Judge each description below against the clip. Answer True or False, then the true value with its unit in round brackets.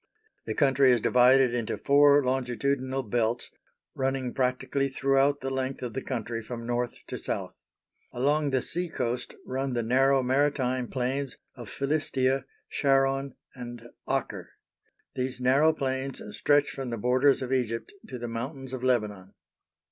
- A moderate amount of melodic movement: False (1.8 semitones)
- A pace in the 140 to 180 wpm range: True (145 wpm)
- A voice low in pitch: True (130 Hz)